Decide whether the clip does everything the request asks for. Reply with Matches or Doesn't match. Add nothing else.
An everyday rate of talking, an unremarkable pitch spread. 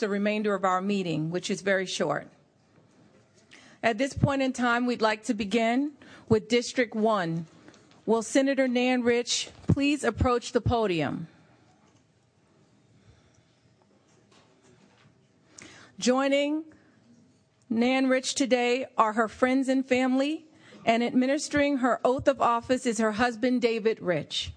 Doesn't match